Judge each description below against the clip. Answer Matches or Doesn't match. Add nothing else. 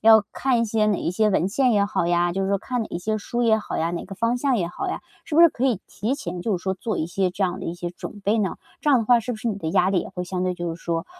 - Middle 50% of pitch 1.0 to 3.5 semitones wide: Doesn't match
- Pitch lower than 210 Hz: Matches